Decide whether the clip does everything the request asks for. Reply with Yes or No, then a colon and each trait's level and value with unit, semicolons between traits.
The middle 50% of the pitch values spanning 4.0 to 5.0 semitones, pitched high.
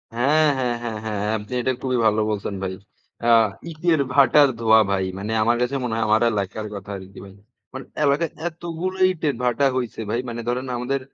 No: average, 4.5 semitones; low, 120 Hz